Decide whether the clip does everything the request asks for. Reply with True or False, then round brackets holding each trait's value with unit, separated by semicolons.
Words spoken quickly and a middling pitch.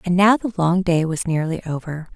True (225 wpm; 175 Hz)